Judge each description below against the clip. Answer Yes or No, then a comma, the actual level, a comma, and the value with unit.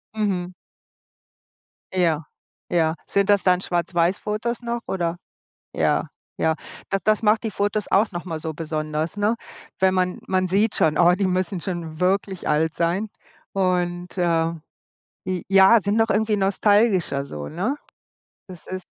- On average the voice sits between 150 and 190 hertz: Yes, medium, 185 Hz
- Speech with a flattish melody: No, average, 3.2 semitones